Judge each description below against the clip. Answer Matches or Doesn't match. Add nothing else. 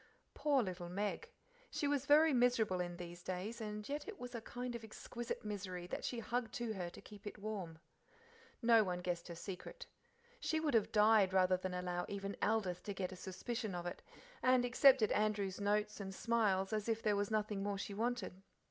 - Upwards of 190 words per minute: Matches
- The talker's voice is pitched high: Matches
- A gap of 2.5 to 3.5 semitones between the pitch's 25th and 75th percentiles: Doesn't match